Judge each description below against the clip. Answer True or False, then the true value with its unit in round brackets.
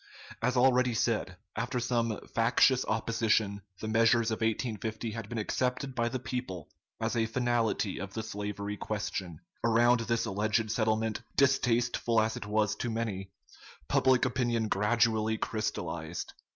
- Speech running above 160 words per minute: False (140 wpm)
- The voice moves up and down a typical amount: False (1.9 semitones)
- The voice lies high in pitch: False (115 Hz)